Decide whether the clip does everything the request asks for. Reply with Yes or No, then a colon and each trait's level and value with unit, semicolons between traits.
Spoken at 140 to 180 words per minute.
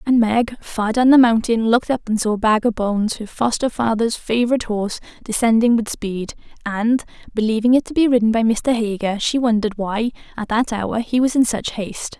No: average, 195 wpm